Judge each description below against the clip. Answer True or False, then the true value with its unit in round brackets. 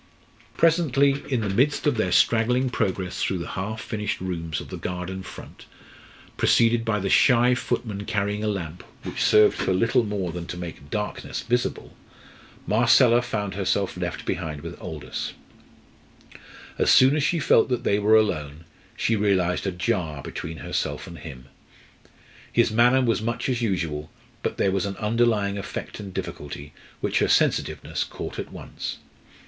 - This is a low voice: True (105 Hz)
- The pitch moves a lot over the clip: False (4.8 semitones)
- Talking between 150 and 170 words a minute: True (160 wpm)